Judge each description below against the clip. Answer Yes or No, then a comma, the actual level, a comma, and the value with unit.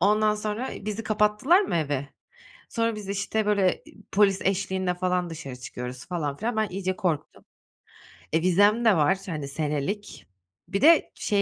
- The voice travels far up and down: No, average, 4.5 semitones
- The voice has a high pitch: Yes, high, 195 Hz